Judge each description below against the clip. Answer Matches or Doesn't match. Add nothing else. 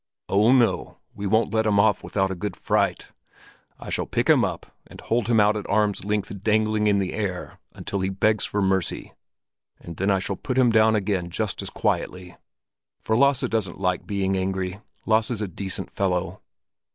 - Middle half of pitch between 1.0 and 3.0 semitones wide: Matches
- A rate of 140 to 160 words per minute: Doesn't match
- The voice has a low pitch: Matches